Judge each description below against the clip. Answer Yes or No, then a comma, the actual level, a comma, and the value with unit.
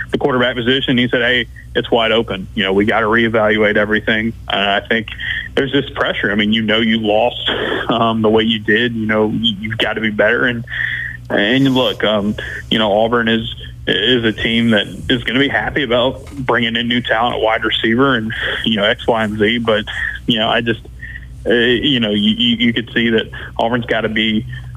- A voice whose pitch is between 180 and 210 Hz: No, low, 110 Hz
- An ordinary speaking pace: No, fast, 215 wpm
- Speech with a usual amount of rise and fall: No, narrow, 2.0 semitones